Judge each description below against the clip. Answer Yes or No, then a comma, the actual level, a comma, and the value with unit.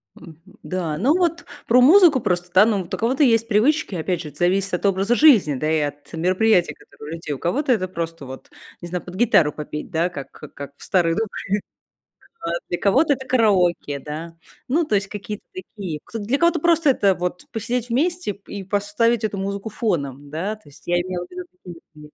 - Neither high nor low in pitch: No, high, 195 Hz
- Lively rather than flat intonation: Yes, wide, 6.0 semitones